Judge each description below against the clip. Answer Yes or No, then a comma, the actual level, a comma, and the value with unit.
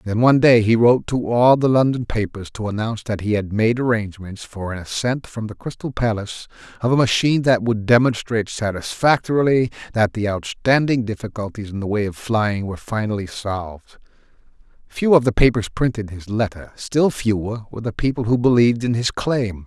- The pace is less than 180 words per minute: No, average, 185 wpm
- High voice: No, low, 110 Hz